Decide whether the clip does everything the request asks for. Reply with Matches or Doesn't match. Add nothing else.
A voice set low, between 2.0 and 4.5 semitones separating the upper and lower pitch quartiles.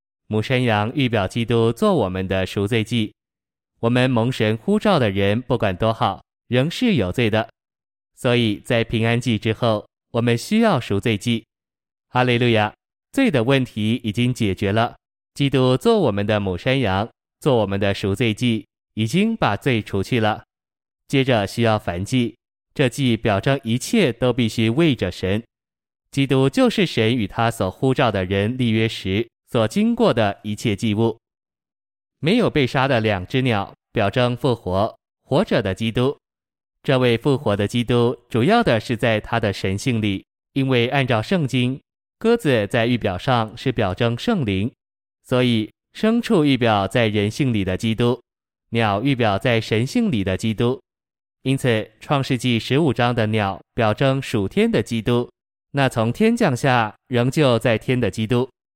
Matches